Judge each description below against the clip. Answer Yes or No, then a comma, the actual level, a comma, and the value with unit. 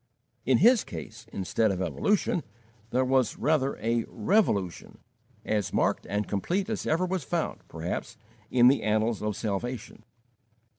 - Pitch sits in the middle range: No, low, 120 Hz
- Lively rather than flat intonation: Yes, wide, 6.9 semitones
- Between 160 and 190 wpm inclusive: No, average, 140 wpm